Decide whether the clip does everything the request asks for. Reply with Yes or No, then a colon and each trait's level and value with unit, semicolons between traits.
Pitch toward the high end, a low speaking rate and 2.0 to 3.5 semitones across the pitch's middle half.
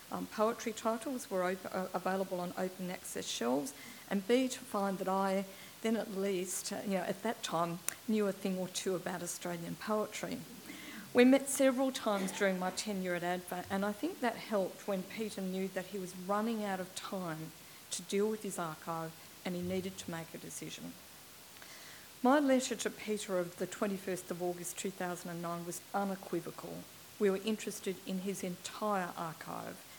No: high, 195 Hz; average, 180 wpm; average, 2.8 semitones